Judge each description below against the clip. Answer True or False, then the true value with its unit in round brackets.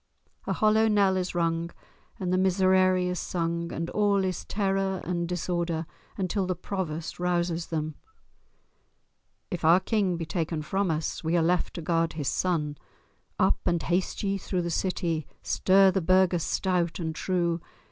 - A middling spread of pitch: False (2.1 semitones)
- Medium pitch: True (180 Hz)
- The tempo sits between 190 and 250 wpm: False (160 wpm)